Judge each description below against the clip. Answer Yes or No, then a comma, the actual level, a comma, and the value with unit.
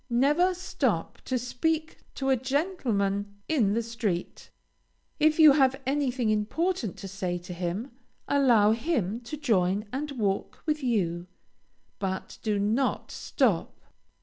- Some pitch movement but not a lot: No, wide, 6.0 semitones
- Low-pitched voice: No, high, 235 Hz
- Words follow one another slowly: Yes, slow, 130 wpm